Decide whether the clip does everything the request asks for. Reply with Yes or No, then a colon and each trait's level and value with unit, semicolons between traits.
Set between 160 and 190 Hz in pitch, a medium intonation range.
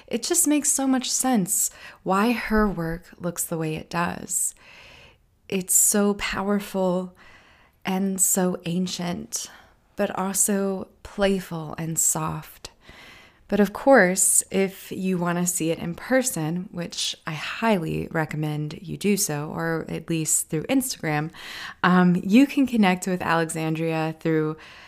Yes: medium, 185 Hz; average, 3.8 semitones